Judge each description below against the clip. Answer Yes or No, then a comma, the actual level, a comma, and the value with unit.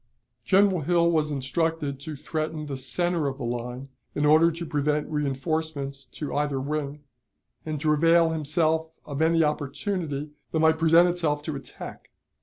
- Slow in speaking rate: No, average, 155 wpm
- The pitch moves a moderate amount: No, narrow, 2.3 semitones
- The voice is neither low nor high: Yes, medium, 155 Hz